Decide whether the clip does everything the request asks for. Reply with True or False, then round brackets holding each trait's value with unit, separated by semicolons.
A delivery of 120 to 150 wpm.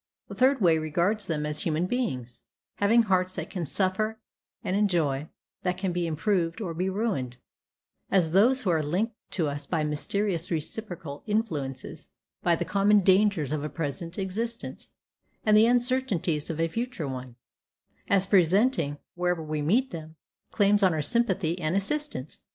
False (160 wpm)